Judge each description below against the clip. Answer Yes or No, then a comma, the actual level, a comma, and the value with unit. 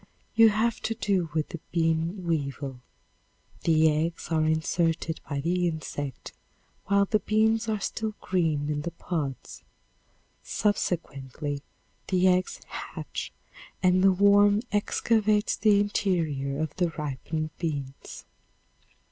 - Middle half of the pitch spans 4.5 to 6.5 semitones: Yes, average, 4.8 semitones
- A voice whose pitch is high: No, medium, 170 Hz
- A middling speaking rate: No, slow, 120 wpm